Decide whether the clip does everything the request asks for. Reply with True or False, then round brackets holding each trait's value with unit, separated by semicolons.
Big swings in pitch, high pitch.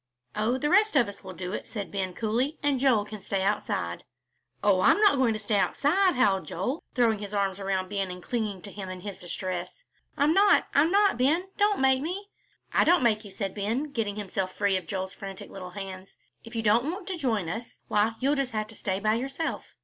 True (6.0 semitones; 215 Hz)